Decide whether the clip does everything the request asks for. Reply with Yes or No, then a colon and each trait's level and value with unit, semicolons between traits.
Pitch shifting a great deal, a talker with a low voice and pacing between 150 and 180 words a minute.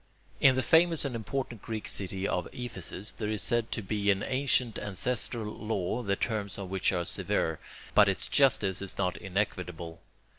No: average, 4.0 semitones; low, 105 Hz; average, 175 wpm